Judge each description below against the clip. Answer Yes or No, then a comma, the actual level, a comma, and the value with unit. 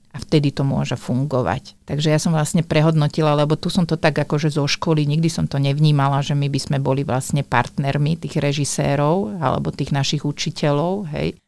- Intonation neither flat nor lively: No, narrow, 2.0 semitones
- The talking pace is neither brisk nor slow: No, fast, 190 wpm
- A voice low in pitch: No, medium, 150 Hz